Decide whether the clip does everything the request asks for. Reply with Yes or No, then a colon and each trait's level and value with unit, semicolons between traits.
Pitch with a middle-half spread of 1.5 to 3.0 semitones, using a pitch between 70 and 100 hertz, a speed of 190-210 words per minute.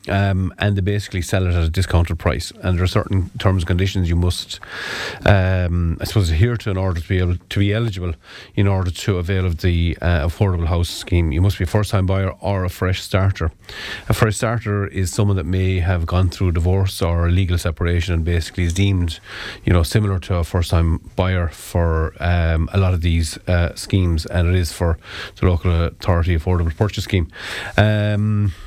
Yes: narrow, 2.5 semitones; very low, 90 Hz; fast, 205 wpm